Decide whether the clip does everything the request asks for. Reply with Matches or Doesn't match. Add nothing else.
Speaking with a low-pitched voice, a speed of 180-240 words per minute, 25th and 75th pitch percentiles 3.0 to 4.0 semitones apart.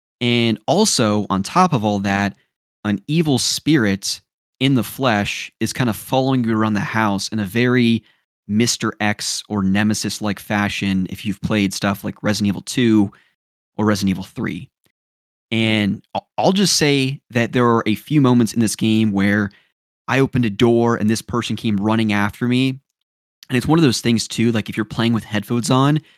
Matches